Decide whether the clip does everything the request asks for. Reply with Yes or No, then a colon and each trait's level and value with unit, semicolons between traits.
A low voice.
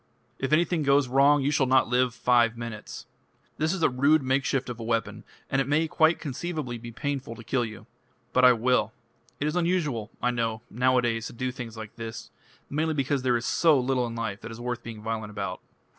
Yes: low, 125 Hz